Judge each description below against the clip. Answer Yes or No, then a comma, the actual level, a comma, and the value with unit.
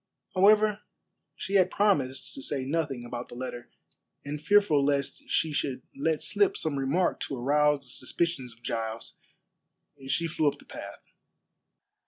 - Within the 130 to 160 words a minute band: Yes, average, 150 wpm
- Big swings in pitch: No, average, 4.8 semitones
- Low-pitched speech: No, medium, 145 Hz